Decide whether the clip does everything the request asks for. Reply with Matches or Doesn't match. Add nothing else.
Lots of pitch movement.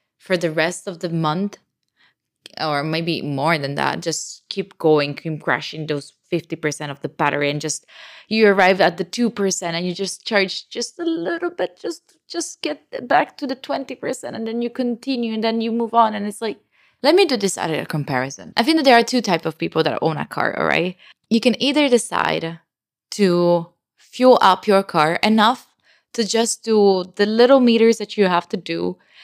Matches